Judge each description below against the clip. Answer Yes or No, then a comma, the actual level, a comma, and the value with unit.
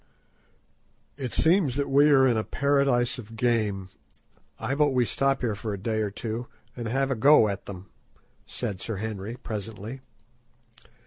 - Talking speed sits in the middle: Yes, average, 155 wpm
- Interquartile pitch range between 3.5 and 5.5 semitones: Yes, average, 4.1 semitones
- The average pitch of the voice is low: Yes, low, 120 Hz